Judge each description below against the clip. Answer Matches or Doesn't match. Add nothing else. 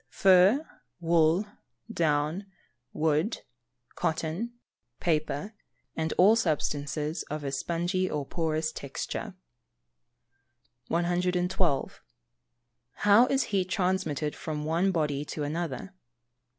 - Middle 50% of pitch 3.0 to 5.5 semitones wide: Matches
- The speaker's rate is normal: Doesn't match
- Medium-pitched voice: Matches